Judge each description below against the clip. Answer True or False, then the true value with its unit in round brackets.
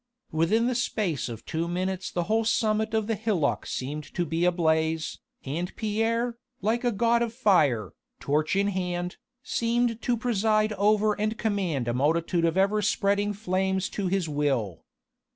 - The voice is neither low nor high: False (195 Hz)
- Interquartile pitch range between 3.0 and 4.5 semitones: False (5.0 semitones)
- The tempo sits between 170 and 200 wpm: False (160 wpm)